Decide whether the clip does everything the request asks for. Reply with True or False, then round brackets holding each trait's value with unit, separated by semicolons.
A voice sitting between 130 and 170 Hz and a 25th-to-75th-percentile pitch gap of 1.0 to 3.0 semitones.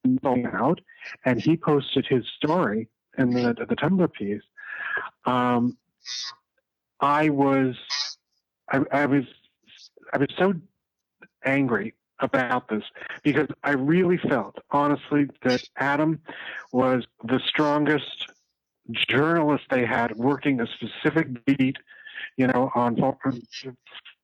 False (140 Hz; 3.4 semitones)